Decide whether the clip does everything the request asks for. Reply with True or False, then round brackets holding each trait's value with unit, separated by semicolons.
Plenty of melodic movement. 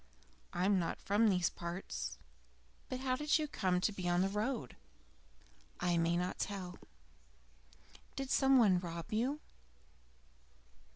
True (6.1 semitones)